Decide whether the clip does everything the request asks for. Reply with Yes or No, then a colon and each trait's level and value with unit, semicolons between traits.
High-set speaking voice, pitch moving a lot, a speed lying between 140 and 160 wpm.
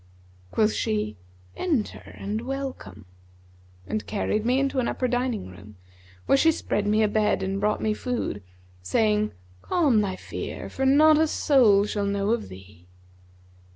No: high, 215 Hz; average, 4.6 semitones; average, 155 wpm